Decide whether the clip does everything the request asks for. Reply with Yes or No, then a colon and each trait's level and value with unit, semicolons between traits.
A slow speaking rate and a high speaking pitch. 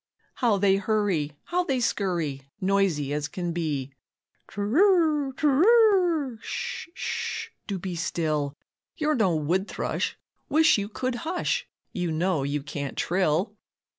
Yes: slow, 130 wpm; high, 195 Hz